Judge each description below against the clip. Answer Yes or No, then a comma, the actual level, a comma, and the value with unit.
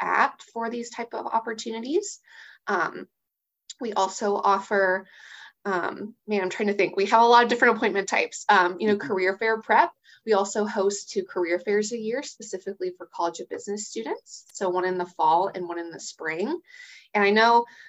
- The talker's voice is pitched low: No, high, 210 Hz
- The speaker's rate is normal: Yes, average, 190 wpm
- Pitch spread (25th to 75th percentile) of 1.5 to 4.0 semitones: Yes, average, 3.4 semitones